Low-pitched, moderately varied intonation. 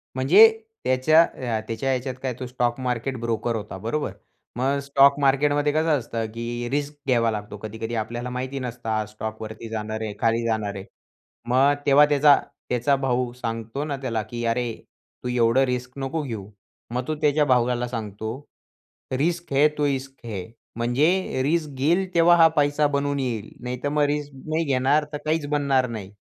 Yes: low, 130 Hz; average, 3.7 semitones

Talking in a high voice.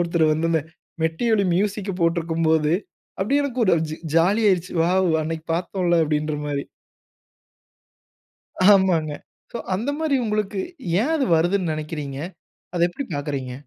No: medium, 170 Hz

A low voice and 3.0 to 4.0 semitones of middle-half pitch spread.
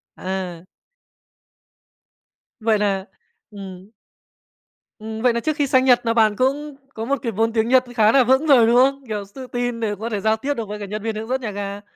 No: high, 225 Hz; average, 3.5 semitones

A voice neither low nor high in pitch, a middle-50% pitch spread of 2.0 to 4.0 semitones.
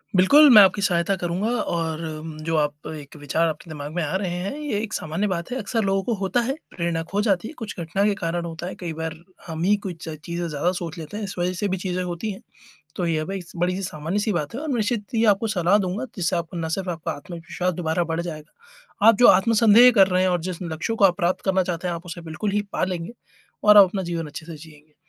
Yes: medium, 180 Hz; average, 3.5 semitones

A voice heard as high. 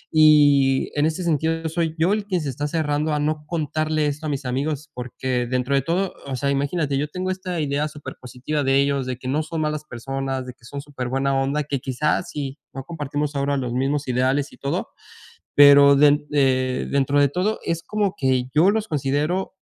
No: medium, 145 Hz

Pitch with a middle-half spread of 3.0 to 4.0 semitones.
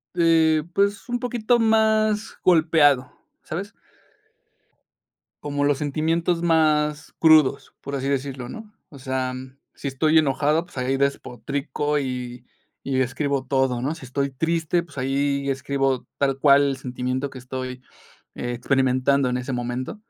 Yes: average, 3.5 semitones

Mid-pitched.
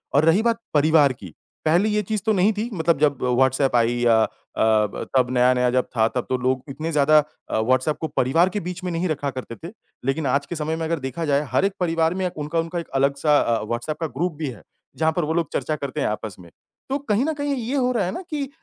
Yes: medium, 155 Hz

